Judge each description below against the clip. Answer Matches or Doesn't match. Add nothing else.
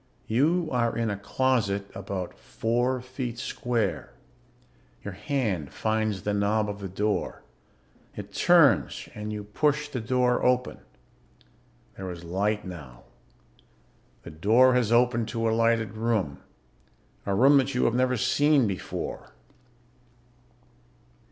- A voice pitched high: Doesn't match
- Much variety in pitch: Doesn't match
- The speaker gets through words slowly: Matches